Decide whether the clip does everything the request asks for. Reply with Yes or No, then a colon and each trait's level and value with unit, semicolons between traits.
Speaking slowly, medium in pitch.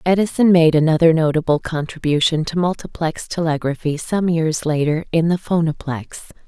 Yes: slow, 130 wpm; medium, 160 Hz